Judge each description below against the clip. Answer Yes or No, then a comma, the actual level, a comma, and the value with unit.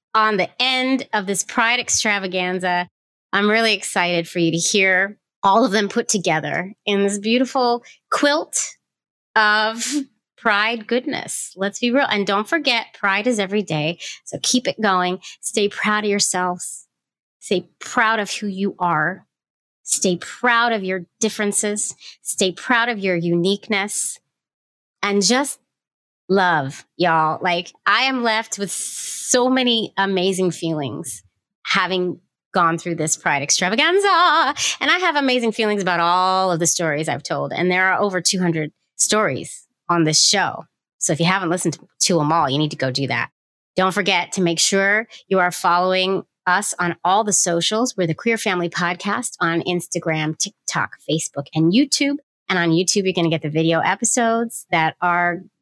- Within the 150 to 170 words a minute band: Yes, average, 165 wpm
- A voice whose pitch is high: Yes, high, 195 Hz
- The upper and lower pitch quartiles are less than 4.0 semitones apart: No, average, 4.3 semitones